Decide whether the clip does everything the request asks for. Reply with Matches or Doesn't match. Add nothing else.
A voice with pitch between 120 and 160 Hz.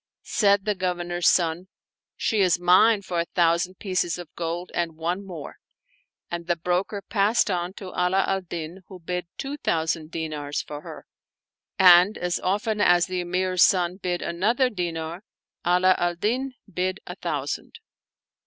Doesn't match